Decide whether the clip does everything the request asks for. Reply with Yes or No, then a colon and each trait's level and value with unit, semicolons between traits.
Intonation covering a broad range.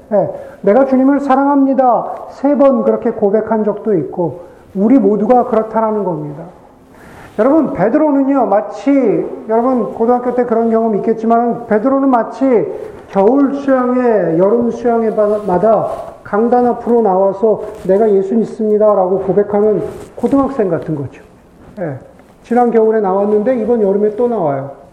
No: average, 3.5 semitones